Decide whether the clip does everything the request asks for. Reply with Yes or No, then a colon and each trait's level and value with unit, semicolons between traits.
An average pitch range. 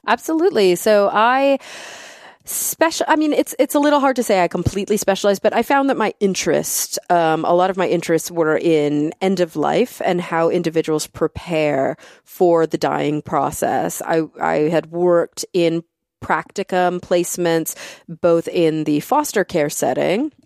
No: wide, 5.8 semitones